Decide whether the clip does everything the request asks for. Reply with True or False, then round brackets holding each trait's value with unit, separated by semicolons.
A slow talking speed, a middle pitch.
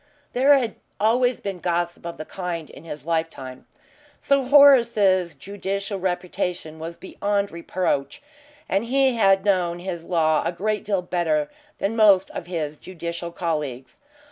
False (145 wpm; 180 Hz)